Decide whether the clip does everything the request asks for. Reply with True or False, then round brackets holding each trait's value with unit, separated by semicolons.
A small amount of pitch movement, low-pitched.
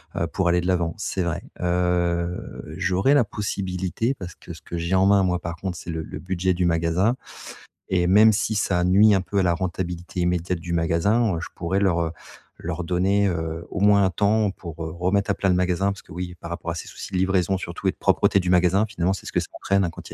True (2.3 semitones; 90 Hz)